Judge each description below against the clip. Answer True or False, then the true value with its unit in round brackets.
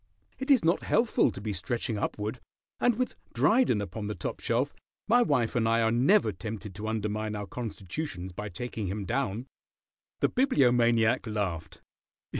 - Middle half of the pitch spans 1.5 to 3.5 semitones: False (4.2 semitones)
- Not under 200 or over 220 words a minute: False (160 wpm)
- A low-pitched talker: True (110 Hz)